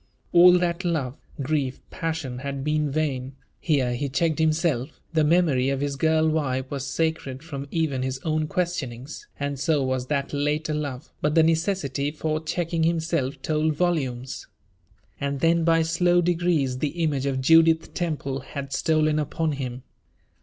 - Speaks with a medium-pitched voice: Yes, medium, 150 Hz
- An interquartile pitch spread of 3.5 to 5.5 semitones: No, average, 3.1 semitones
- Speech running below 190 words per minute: Yes, average, 155 wpm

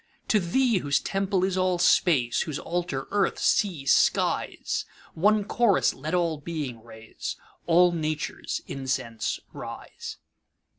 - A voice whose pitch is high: No, medium, 170 Hz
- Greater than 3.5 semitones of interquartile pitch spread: Yes, average, 5.2 semitones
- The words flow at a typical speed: No, slow, 105 wpm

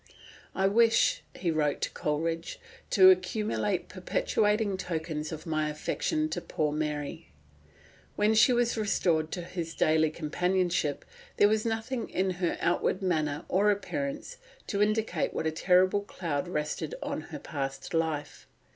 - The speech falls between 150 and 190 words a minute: No, average, 140 wpm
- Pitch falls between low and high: Yes, medium, 180 Hz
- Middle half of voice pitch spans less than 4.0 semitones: No, average, 4.9 semitones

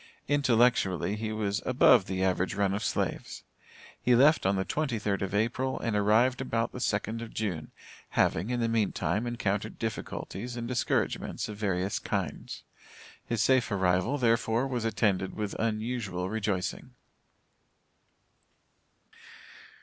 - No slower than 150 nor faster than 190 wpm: No, slow, 135 wpm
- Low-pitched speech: Yes, low, 110 Hz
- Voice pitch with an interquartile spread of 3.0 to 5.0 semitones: Yes, average, 3.4 semitones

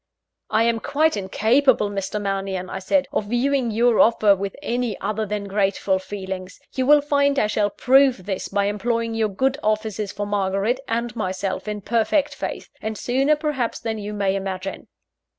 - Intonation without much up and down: No, average, 3.7 semitones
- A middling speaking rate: Yes, average, 170 wpm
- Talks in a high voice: Yes, high, 215 Hz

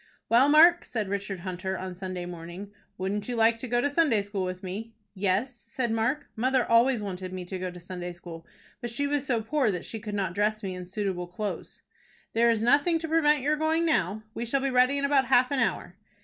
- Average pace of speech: No, fast, 225 wpm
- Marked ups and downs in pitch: Yes, wide, 5.9 semitones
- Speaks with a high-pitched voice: Yes, high, 220 Hz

